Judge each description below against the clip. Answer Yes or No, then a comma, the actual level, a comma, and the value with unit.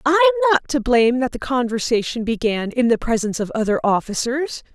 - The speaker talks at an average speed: Yes, average, 175 wpm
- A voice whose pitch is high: Yes, very high, 260 Hz